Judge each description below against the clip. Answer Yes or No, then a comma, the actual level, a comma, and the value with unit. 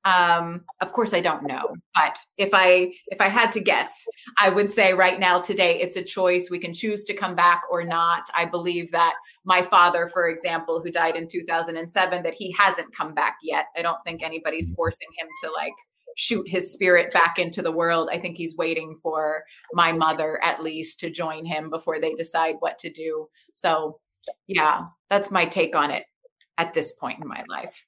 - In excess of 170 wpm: Yes, average, 200 wpm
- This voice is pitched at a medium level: Yes, medium, 175 Hz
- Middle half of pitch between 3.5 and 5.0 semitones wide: No, narrow, 2.6 semitones